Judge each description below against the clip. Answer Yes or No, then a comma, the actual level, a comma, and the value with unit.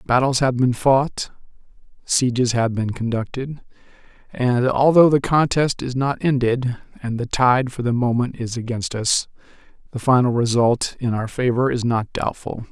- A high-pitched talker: No, low, 125 Hz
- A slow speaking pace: No, average, 155 wpm